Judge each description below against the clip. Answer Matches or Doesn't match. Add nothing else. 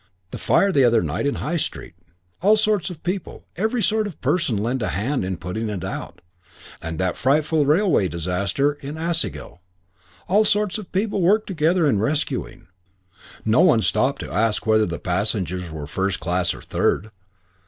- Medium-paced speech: Matches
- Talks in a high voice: Doesn't match